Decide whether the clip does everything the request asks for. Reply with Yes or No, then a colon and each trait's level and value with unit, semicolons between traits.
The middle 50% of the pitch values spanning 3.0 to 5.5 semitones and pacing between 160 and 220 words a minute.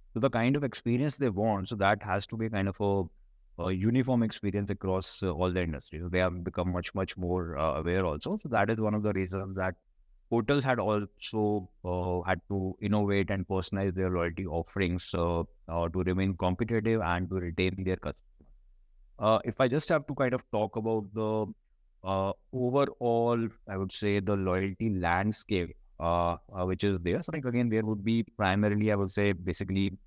Yes: average, 3.4 semitones; average, 195 wpm